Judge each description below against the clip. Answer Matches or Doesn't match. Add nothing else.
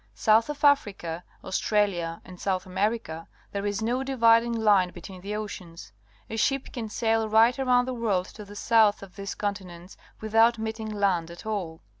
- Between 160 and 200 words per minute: Matches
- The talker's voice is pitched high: Matches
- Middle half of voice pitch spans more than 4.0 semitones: Doesn't match